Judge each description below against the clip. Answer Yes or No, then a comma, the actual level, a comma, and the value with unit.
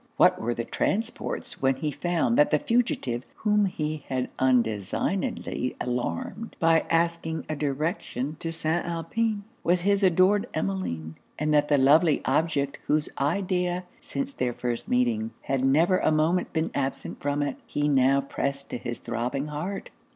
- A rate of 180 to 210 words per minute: No, average, 155 wpm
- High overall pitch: No, medium, 155 Hz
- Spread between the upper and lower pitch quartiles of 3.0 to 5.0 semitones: No, wide, 5.4 semitones